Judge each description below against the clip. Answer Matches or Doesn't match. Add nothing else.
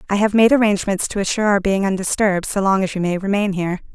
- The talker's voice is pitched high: Matches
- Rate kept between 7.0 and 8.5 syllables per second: Matches